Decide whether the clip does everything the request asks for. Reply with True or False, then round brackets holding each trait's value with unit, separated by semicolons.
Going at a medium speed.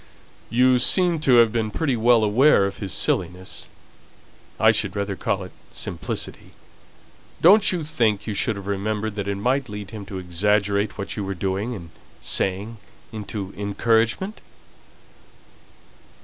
True (145 wpm)